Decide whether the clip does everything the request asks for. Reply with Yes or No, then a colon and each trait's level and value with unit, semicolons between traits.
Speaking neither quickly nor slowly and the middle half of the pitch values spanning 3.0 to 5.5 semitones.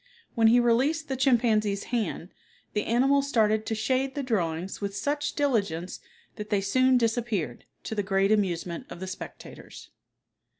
Yes: average, 155 wpm; average, 4.6 semitones